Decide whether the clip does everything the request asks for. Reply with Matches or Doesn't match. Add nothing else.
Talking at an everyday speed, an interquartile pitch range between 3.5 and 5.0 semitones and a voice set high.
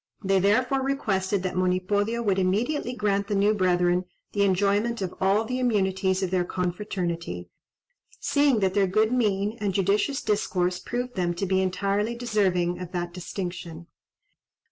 Doesn't match